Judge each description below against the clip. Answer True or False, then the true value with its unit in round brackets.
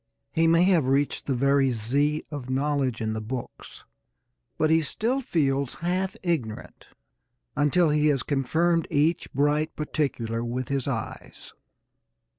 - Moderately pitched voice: True (145 Hz)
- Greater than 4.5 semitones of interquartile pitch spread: False (3.8 semitones)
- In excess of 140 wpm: False (135 wpm)